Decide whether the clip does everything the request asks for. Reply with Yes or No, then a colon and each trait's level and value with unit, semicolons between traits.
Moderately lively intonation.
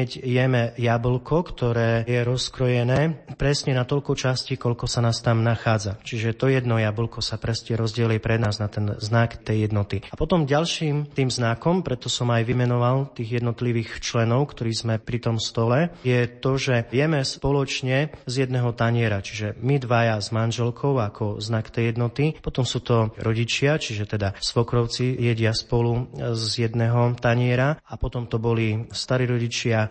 No: narrow, 2.1 semitones